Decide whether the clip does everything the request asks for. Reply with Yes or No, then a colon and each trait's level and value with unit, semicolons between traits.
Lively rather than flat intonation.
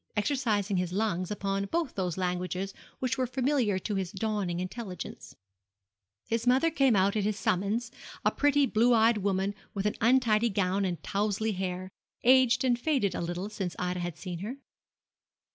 No: average, 4.2 semitones